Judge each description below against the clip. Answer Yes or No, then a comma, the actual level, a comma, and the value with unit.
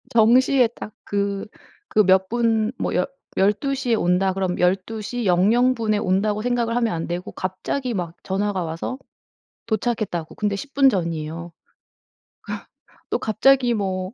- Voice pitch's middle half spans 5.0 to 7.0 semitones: No, average, 4.1 semitones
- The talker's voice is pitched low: No, high, 210 Hz